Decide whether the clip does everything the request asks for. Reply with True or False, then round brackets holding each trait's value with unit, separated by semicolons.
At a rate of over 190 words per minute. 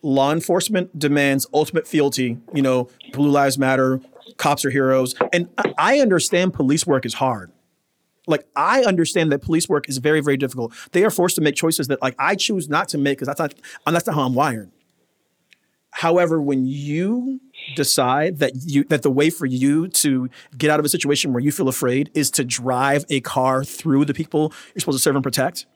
True (200 wpm)